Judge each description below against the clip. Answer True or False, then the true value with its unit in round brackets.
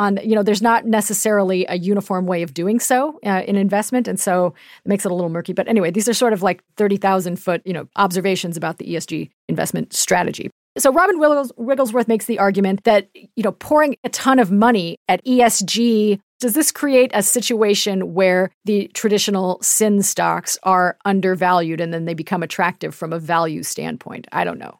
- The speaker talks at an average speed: True (195 wpm)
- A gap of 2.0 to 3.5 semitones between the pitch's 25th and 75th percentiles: False (3.9 semitones)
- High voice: True (200 Hz)